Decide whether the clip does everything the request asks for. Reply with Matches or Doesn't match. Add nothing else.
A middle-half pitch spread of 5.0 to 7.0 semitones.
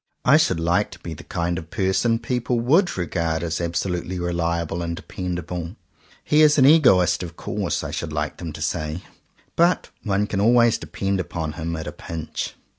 Doesn't match